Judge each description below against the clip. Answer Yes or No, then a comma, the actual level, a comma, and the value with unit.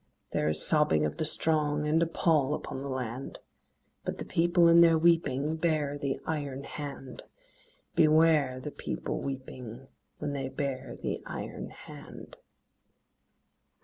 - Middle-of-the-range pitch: Yes, medium, 145 Hz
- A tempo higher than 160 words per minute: No, average, 140 wpm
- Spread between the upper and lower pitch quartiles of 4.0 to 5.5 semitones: No, average, 3.2 semitones